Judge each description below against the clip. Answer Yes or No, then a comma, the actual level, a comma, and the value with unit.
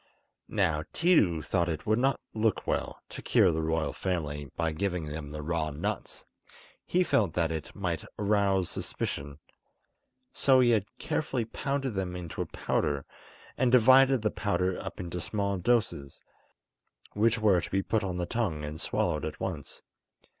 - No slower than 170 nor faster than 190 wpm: No, average, 160 wpm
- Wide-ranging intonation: Yes, wide, 5.7 semitones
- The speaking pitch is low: Yes, very low, 95 Hz